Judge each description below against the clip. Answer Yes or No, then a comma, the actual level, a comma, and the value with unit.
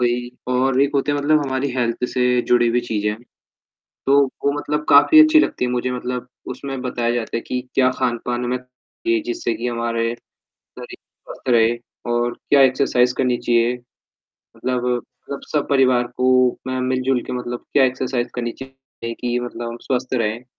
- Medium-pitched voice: No, low, 125 Hz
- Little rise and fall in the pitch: Yes, narrow, 1.7 semitones